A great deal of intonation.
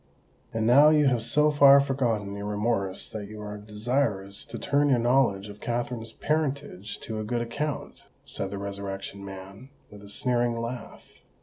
No: average, 4.6 semitones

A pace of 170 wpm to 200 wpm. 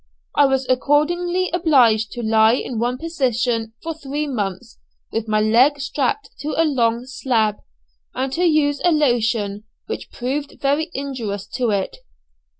No: average, 150 wpm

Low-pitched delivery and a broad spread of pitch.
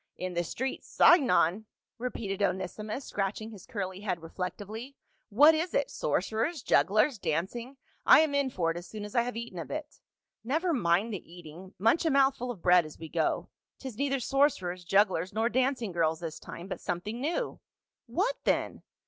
No: high, 215 Hz; wide, 6.7 semitones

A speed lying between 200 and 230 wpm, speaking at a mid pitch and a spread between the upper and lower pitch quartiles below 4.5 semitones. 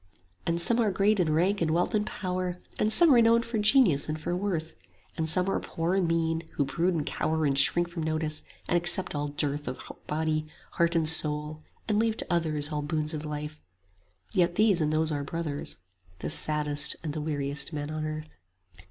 Yes: fast, 205 wpm; medium, 160 Hz; average, 3.1 semitones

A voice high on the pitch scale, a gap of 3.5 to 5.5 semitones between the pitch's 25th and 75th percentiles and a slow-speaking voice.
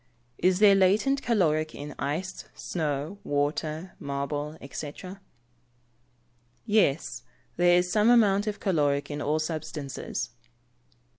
No: medium, 160 Hz; average, 5.0 semitones; slow, 105 wpm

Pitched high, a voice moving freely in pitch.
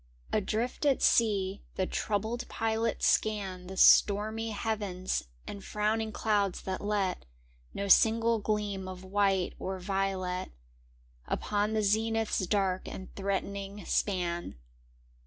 No: high, 205 Hz; narrow, 2.4 semitones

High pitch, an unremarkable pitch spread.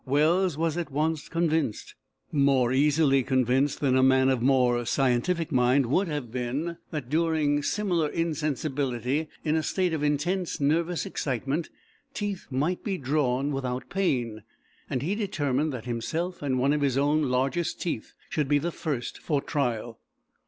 No: medium, 145 Hz; average, 3.8 semitones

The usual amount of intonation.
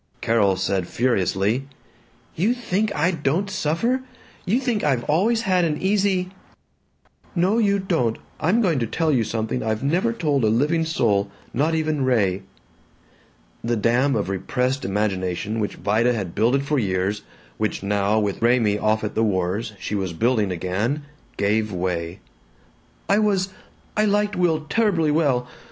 No: wide, 8.8 semitones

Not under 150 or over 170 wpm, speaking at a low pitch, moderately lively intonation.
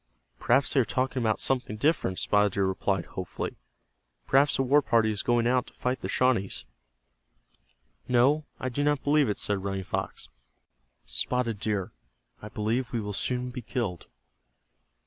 Yes: average, 160 wpm; low, 120 Hz; average, 4.1 semitones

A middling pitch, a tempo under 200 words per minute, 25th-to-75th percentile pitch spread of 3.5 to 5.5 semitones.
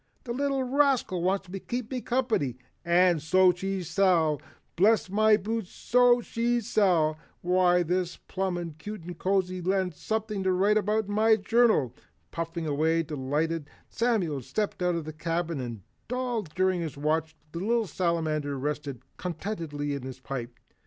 Yes: medium, 180 Hz; average, 155 wpm; average, 5.2 semitones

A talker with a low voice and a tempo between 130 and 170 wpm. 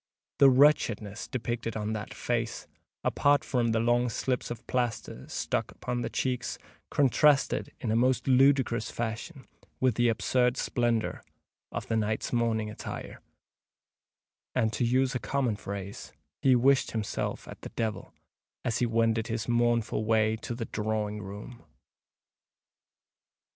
Yes: low, 120 Hz; average, 140 wpm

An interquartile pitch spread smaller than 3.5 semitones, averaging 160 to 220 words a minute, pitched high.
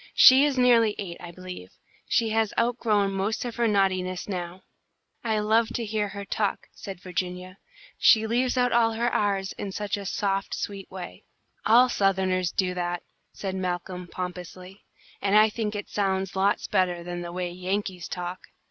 Yes: average, 3.1 semitones; average, 175 wpm; high, 195 Hz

